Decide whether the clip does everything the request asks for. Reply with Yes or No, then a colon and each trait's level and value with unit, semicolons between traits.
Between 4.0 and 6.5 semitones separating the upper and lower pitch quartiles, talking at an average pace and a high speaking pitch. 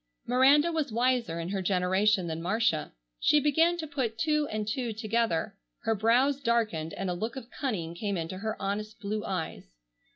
Yes: wide, 5.4 semitones; average, 175 wpm; high, 220 Hz